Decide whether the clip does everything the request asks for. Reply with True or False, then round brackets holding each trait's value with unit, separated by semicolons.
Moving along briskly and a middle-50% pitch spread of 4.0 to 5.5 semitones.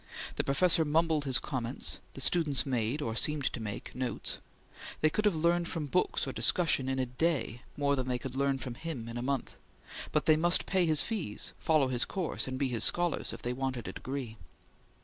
True (210 wpm; 4.3 semitones)